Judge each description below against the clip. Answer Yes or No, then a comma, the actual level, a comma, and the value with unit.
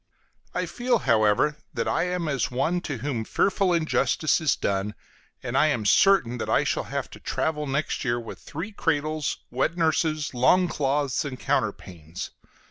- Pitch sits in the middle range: Yes, medium, 145 Hz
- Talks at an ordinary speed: Yes, average, 165 wpm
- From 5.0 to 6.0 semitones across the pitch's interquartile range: Yes, average, 5.3 semitones